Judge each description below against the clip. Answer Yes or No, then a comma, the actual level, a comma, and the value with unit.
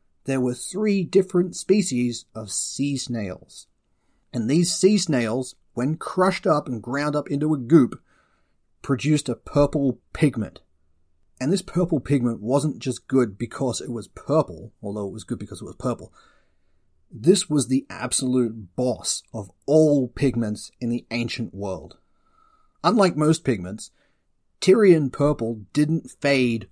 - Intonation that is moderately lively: No, wide, 5.7 semitones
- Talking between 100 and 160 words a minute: Yes, average, 140 wpm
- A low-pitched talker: Yes, low, 130 Hz